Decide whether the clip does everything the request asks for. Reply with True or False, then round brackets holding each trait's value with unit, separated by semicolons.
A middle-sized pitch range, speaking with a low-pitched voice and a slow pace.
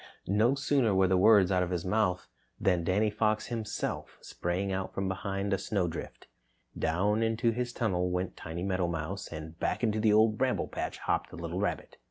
False (3.2 semitones; 95 Hz; 185 wpm)